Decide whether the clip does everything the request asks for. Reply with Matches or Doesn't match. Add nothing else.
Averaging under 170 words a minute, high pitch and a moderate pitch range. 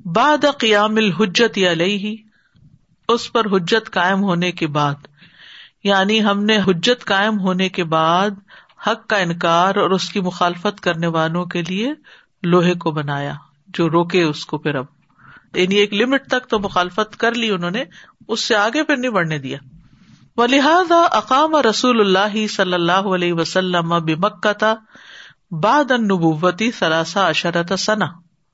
Matches